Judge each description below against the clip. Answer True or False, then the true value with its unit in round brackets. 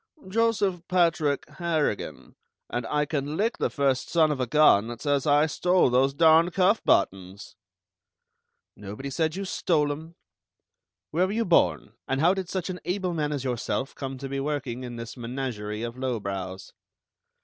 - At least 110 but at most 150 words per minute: False (165 wpm)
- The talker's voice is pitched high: False (145 Hz)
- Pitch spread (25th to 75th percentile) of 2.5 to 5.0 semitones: False (5.5 semitones)